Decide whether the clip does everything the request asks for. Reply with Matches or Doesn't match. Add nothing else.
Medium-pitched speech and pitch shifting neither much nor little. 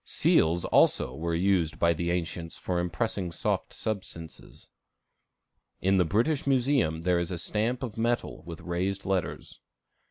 Doesn't match